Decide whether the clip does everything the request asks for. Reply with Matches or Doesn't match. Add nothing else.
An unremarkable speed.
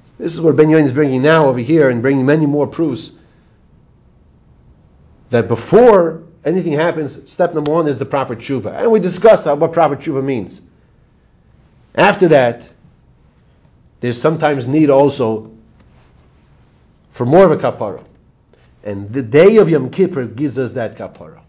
Matches